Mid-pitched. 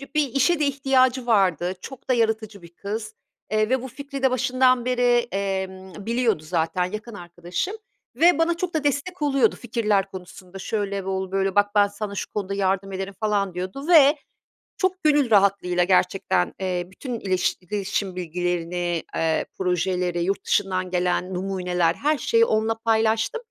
No: high, 200 Hz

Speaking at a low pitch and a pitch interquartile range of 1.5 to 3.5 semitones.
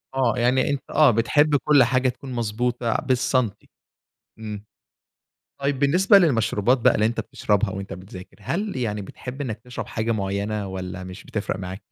No: low, 115 Hz; average, 4.2 semitones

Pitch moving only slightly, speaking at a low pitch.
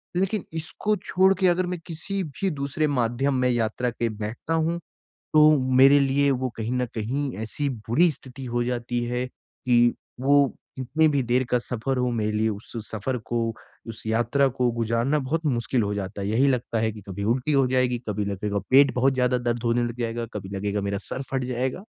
No: average, 3.4 semitones; low, 125 Hz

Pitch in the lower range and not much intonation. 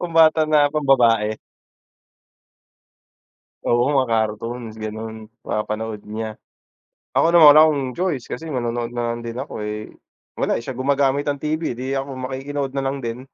No: low, 130 Hz; average, 4.1 semitones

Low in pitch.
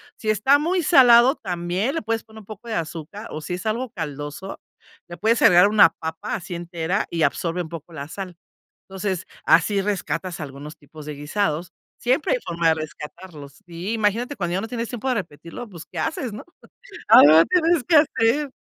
No: high, 190 Hz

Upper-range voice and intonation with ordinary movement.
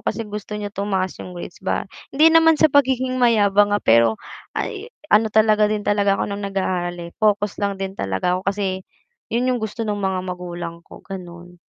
Yes: high, 200 Hz; average, 3.1 semitones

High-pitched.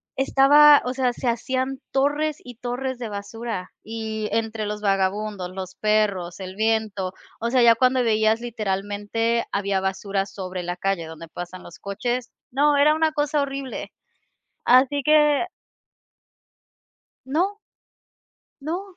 Yes: high, 225 Hz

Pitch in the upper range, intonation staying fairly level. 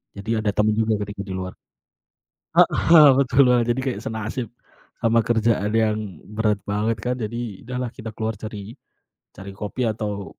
No: low, 110 Hz; narrow, 2.2 semitones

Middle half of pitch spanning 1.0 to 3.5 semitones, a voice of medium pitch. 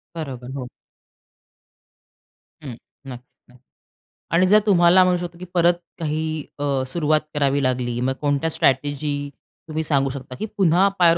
No: average, 4.2 semitones; medium, 150 Hz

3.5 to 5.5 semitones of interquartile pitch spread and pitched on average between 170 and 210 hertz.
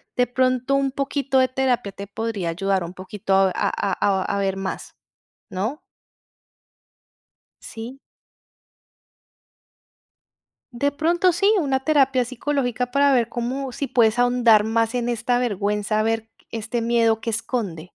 No: average, 4.0 semitones; high, 235 Hz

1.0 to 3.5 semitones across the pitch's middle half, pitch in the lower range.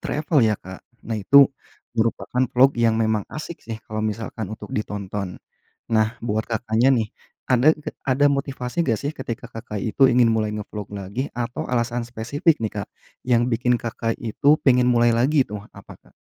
Yes: narrow, 2.6 semitones; low, 115 Hz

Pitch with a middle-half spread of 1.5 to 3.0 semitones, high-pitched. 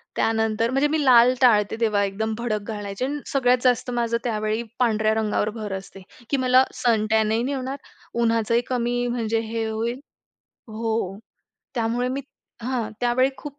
Yes: narrow, 2.5 semitones; high, 230 Hz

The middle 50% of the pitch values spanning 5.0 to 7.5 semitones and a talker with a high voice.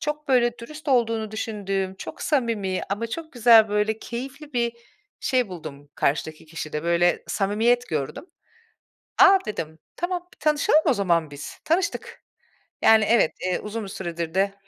Yes: wide, 5.6 semitones; high, 220 Hz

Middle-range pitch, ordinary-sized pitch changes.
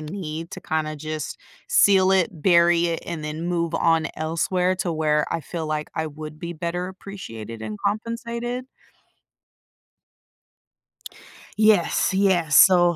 Yes: medium, 170 Hz; average, 3.3 semitones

